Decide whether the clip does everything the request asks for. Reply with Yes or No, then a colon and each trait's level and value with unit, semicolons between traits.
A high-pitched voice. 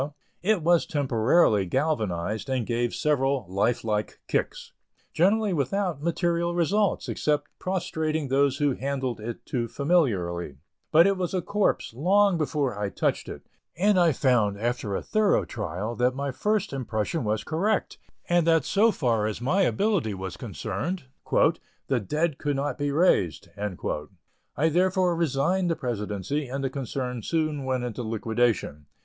No: medium, 140 Hz